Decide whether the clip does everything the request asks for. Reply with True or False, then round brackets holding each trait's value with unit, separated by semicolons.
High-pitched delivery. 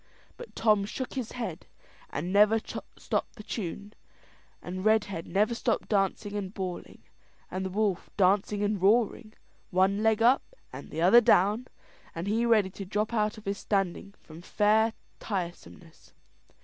True (205 Hz)